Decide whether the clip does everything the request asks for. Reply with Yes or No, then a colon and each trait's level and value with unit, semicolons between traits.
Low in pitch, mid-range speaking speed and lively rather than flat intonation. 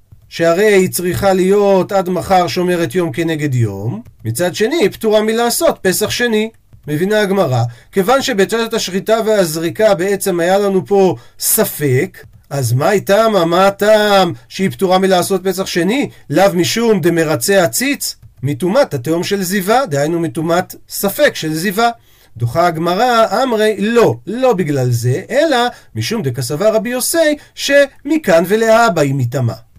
No: high, 190 Hz; average, 135 wpm; wide, 6.0 semitones